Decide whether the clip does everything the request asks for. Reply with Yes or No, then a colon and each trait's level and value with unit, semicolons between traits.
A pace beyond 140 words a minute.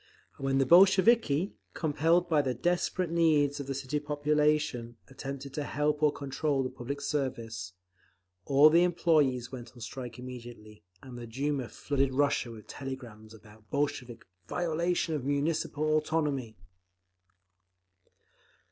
No: slow, 135 wpm